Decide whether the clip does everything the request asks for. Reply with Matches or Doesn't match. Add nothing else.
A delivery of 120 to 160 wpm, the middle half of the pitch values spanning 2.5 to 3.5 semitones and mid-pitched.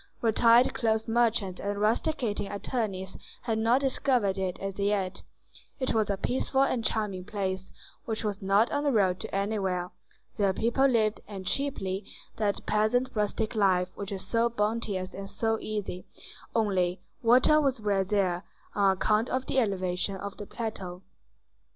Doesn't match